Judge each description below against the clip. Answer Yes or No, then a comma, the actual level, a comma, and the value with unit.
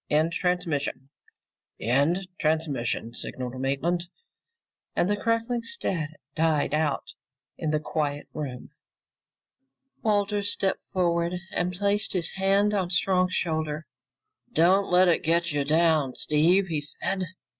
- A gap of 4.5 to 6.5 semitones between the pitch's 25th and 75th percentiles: No, average, 4.0 semitones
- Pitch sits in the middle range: Yes, medium, 170 Hz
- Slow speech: Yes, slow, 120 wpm